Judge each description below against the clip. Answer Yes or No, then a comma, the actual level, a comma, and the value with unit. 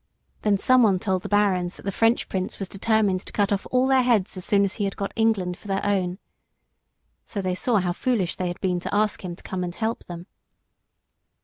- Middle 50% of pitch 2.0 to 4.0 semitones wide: Yes, average, 3.0 semitones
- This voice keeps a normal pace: No, fast, 225 wpm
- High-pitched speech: Yes, high, 195 Hz